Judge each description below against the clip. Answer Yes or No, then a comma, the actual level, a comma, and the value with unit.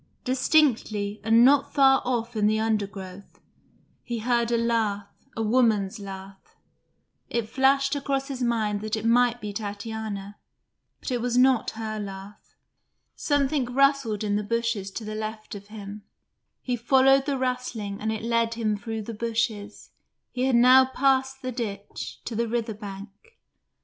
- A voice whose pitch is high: Yes, high, 225 Hz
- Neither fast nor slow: Yes, average, 155 wpm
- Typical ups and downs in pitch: Yes, average, 3.3 semitones